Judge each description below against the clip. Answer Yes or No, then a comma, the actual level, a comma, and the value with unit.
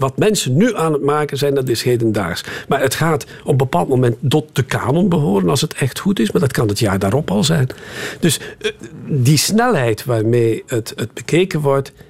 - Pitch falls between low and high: Yes, medium, 145 Hz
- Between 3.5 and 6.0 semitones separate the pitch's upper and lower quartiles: Yes, average, 4.2 semitones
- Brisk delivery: Yes, fast, 210 wpm